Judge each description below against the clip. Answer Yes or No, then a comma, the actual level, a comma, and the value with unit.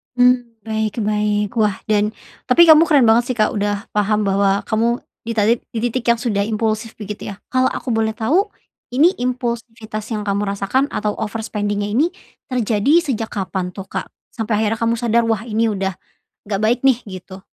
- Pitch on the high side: Yes, high, 220 Hz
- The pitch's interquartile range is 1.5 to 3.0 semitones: Yes, narrow, 2.5 semitones